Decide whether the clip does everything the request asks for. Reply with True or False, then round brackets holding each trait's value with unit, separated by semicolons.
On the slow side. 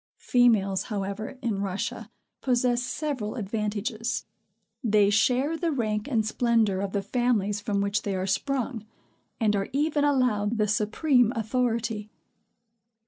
True (130 wpm)